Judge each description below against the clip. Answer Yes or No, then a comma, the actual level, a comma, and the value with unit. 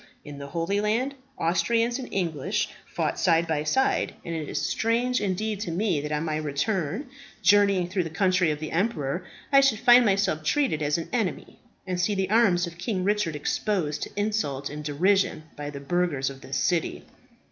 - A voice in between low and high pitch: Yes, medium, 180 Hz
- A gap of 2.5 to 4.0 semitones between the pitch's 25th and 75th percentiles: No, wide, 5.5 semitones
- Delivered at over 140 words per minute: Yes, average, 190 wpm